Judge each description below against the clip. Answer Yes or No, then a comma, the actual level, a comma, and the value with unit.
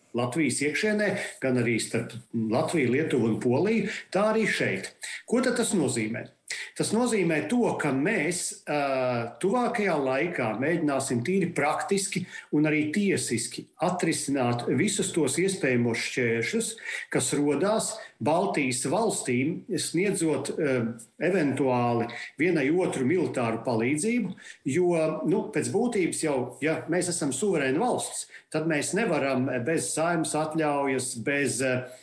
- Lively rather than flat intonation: Yes, wide, 6.7 semitones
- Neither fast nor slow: No, slow, 120 wpm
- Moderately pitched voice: Yes, medium, 150 Hz